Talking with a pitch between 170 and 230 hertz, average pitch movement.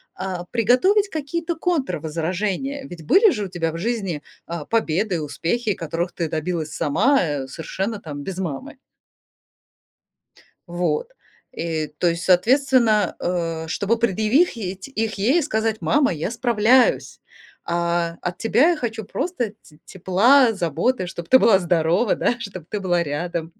No: high, 190 Hz; wide, 6.1 semitones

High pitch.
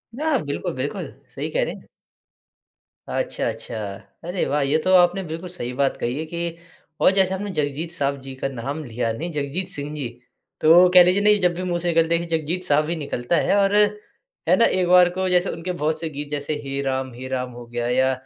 No: medium, 160 Hz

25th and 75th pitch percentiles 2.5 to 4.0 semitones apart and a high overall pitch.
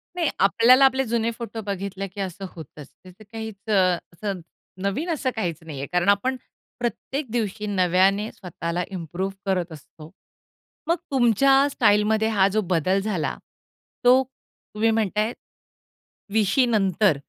Yes: average, 3.7 semitones; high, 205 Hz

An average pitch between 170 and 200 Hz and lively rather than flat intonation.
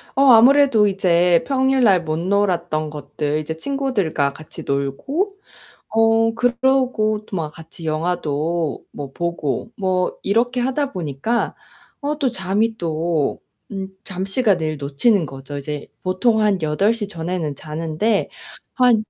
Yes: medium, 185 Hz; wide, 6.7 semitones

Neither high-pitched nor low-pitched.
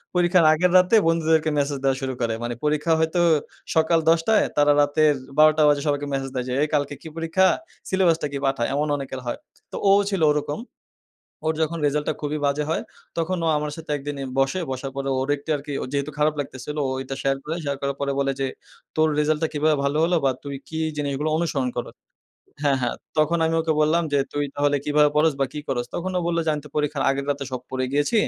Yes: medium, 150 Hz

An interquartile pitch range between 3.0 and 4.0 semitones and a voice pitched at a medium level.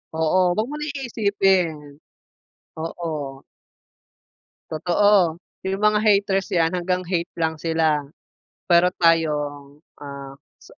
Yes: average, 3.6 semitones; medium, 170 Hz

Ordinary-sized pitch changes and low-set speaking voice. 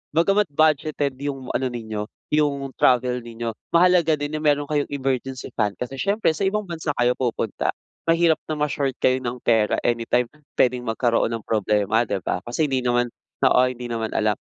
Yes: average, 4.2 semitones; low, 130 Hz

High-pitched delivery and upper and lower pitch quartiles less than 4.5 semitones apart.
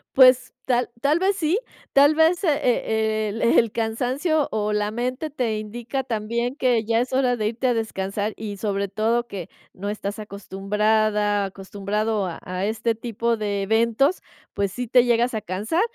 Yes: high, 225 Hz; average, 3.2 semitones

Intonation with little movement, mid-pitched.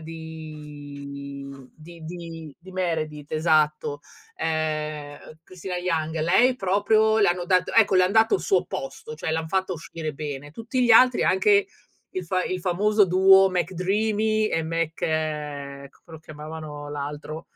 No: average, 3.8 semitones; medium, 165 Hz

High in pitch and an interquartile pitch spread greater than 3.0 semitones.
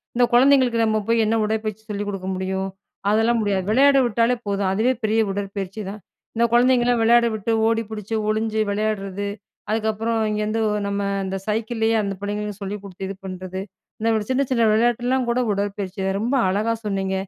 No: high, 215 Hz; narrow, 2.5 semitones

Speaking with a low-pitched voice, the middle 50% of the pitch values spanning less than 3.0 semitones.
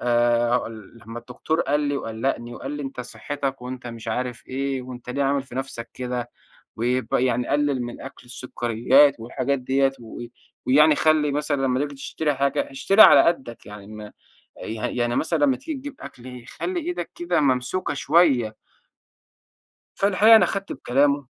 No: low, 130 Hz; average, 3.3 semitones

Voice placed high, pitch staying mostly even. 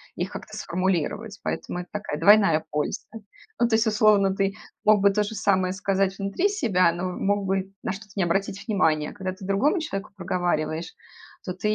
Yes: high, 195 Hz; narrow, 2.2 semitones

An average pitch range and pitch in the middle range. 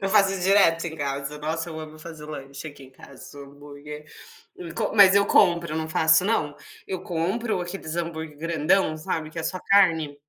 Yes: average, 3.4 semitones; medium, 160 Hz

